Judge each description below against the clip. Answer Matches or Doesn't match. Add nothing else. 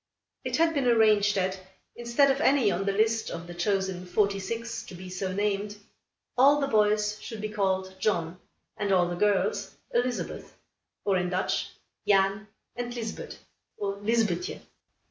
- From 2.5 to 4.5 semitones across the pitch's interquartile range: Matches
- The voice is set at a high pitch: Matches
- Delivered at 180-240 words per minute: Doesn't match